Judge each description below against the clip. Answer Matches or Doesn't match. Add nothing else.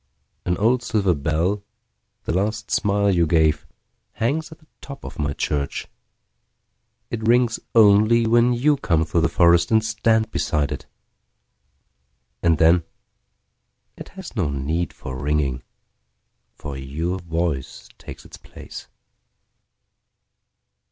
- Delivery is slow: Matches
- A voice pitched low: Matches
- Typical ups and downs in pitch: Doesn't match